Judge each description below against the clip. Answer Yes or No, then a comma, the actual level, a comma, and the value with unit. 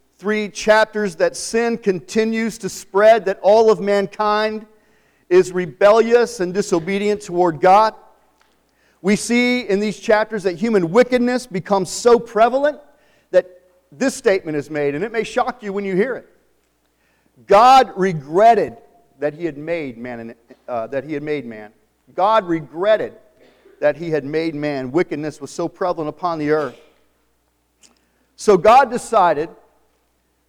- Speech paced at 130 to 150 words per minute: Yes, average, 140 wpm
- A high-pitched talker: Yes, high, 195 Hz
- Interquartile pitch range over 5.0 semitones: Yes, wide, 5.6 semitones